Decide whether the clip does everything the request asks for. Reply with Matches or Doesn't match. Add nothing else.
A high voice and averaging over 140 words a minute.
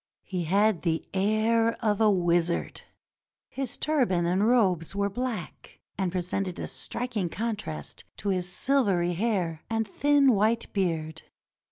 Doesn't match